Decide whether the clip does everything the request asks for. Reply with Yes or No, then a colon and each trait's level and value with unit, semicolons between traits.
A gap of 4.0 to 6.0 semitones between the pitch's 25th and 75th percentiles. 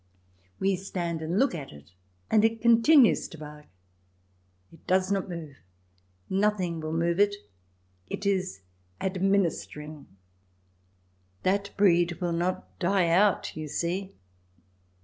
No: average, 3.2 semitones